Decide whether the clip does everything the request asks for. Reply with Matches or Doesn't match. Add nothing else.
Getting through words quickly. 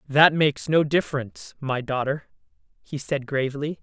Doesn't match